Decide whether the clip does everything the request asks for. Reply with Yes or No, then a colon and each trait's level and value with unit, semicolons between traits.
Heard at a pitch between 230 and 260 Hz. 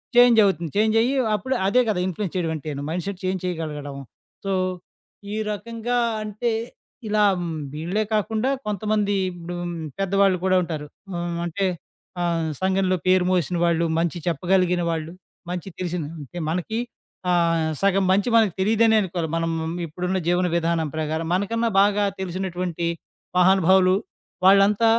No: medium, 185 Hz